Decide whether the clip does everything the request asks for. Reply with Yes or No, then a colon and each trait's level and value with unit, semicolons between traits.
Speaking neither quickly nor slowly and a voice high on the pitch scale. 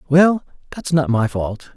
No: average, 170 wpm; medium, 140 Hz